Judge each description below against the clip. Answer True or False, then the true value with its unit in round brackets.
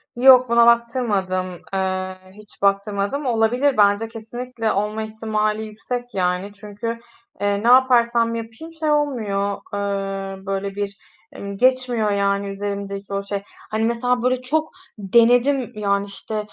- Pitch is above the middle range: True (215 Hz)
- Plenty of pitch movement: False (3.2 semitones)